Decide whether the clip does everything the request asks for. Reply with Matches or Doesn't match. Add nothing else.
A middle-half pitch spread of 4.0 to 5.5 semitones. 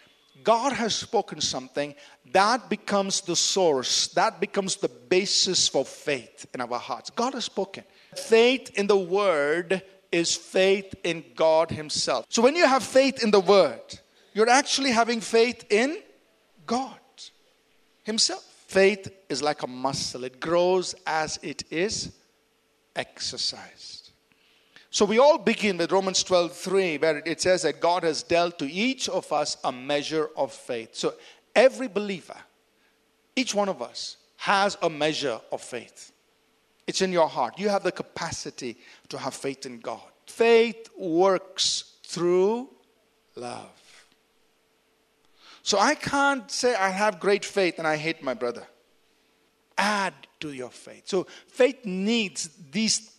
Matches